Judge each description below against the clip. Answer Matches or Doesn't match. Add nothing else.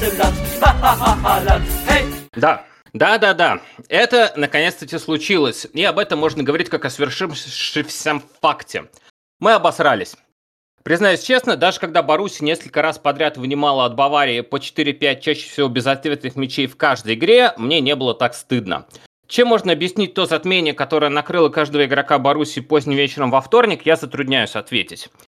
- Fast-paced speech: Doesn't match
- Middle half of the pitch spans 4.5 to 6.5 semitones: Doesn't match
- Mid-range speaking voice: Matches